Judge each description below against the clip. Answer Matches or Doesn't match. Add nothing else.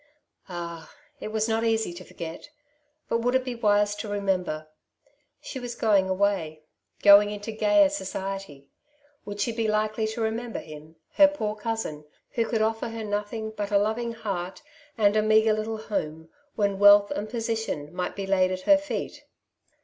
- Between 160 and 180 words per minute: Matches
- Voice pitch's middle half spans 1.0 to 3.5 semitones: Matches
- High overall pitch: Matches